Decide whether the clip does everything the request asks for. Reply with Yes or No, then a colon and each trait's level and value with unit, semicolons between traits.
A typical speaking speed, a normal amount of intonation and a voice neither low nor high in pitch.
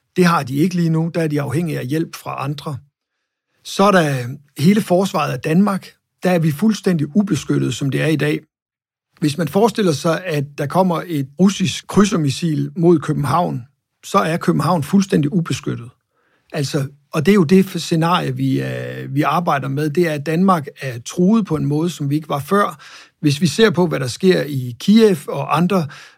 Yes: average, 195 wpm; average, 4.1 semitones; medium, 160 Hz